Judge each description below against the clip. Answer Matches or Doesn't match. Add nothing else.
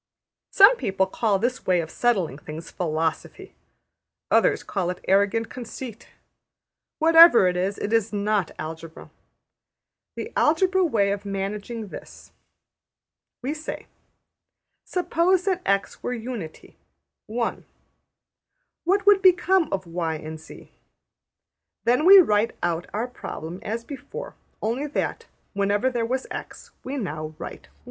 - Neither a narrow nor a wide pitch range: Doesn't match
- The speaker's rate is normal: Doesn't match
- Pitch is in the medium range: Doesn't match